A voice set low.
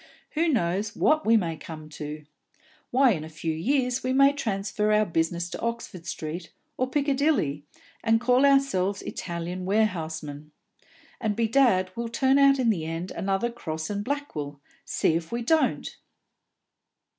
No: high, 205 Hz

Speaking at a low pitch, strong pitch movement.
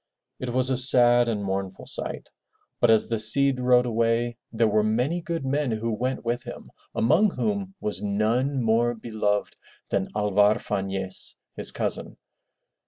No: low, 115 Hz; average, 3.3 semitones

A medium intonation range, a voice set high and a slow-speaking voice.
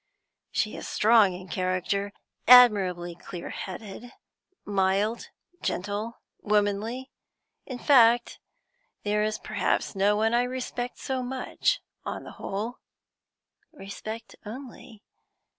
Yes: average, 3.5 semitones; high, 215 Hz; slow, 105 wpm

